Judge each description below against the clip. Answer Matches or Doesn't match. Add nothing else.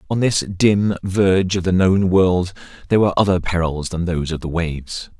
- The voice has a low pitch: Matches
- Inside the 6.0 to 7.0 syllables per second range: Doesn't match